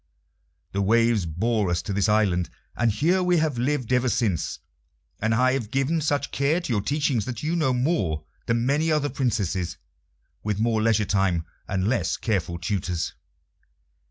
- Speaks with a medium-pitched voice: No, low, 115 Hz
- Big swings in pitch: Yes, wide, 5.8 semitones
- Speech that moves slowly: No, average, 165 wpm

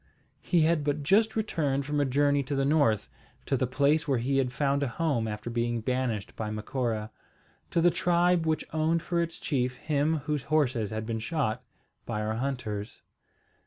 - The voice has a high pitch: No, medium, 140 Hz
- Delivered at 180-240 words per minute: Yes, average, 185 wpm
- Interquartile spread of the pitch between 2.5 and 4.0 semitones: No, average, 4.8 semitones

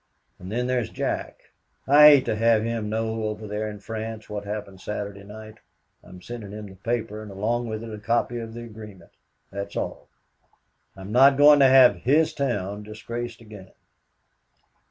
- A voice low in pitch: Yes, low, 110 Hz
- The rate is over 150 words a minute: Yes, average, 175 wpm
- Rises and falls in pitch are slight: Yes, narrow, 2.3 semitones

